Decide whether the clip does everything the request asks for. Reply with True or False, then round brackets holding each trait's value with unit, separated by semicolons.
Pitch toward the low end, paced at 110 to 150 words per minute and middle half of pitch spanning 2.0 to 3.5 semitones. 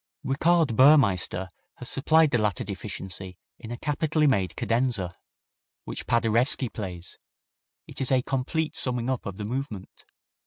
False (120 Hz; 140 wpm; 5.4 semitones)